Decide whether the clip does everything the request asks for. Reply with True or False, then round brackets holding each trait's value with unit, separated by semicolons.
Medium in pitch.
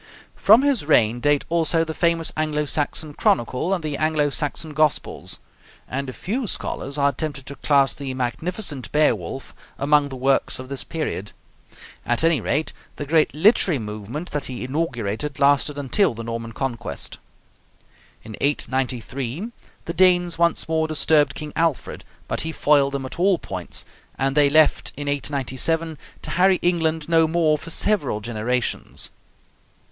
True (145 Hz)